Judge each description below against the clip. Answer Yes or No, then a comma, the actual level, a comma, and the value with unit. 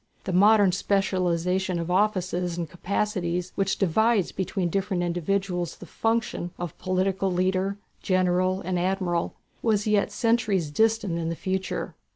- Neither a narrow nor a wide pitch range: No, narrow, 2.1 semitones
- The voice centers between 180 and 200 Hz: Yes, medium, 185 Hz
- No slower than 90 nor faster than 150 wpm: Yes, slow, 135 wpm